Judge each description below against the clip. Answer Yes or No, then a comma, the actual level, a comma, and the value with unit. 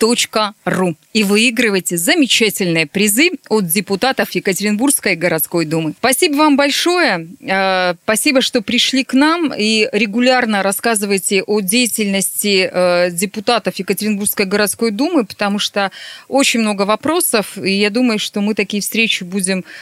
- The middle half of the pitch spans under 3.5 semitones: No, average, 3.9 semitones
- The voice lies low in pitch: No, high, 210 Hz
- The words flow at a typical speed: Yes, average, 120 wpm